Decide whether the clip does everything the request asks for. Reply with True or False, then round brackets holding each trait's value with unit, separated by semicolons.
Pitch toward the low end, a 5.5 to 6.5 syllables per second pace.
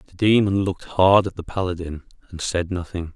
True (90 Hz; 5.7 syllables/s)